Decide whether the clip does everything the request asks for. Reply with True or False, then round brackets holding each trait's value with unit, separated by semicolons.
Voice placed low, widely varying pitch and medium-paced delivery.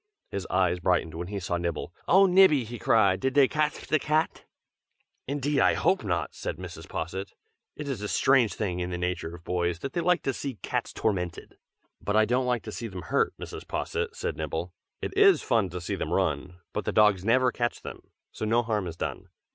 False (110 Hz; 7.4 semitones; 215 wpm)